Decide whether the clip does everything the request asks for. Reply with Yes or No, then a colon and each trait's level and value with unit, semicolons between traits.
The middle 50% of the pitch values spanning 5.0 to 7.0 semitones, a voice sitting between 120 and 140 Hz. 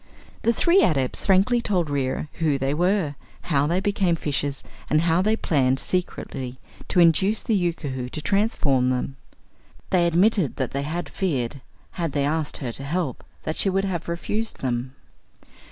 No: wide, 5.4 semitones; medium, 160 Hz